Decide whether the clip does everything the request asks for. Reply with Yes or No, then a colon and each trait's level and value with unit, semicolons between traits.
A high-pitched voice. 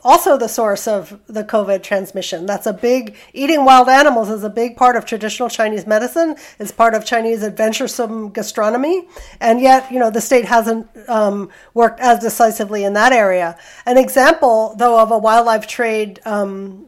Yes: high, 225 Hz